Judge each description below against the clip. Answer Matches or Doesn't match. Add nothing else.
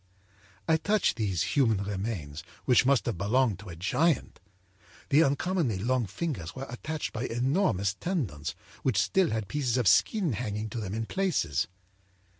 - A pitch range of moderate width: Doesn't match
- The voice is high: Doesn't match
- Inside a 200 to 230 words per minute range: Doesn't match